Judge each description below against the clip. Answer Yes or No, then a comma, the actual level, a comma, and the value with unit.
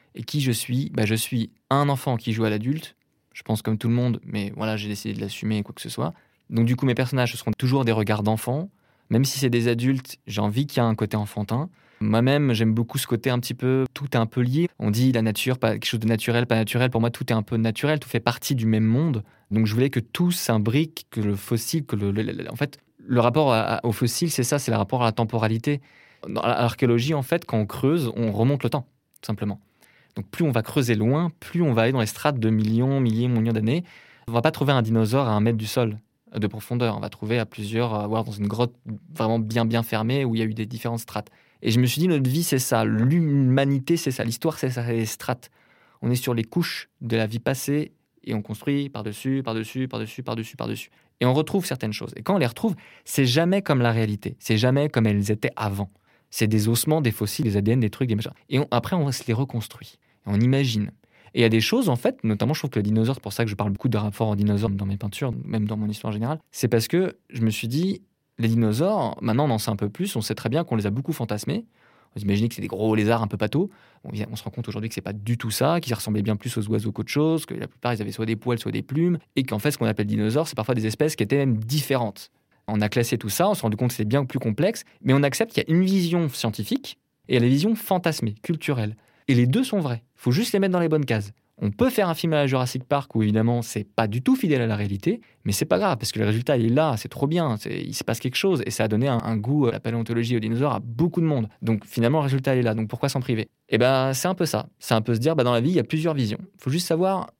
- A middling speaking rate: No, fast, 285 wpm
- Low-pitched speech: Yes, low, 120 Hz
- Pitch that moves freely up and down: No, average, 4.1 semitones